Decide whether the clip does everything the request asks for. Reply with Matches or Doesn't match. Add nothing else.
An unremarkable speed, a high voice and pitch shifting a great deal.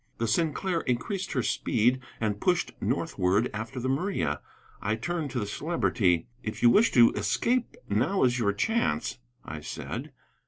Doesn't match